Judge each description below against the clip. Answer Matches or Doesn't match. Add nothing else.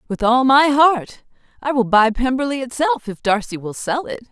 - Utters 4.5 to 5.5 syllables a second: Matches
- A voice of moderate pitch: Doesn't match